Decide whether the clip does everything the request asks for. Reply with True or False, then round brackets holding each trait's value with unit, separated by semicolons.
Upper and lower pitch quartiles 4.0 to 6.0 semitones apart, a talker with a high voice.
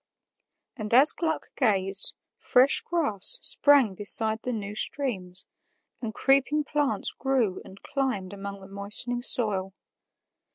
True (5.4 semitones; 220 Hz)